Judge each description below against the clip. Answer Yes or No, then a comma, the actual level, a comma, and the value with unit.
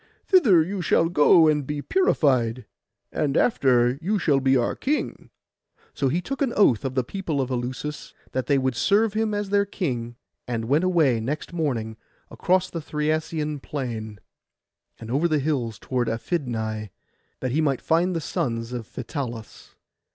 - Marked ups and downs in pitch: Yes, wide, 5.9 semitones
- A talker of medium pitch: Yes, medium, 145 Hz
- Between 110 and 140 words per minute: No, average, 165 wpm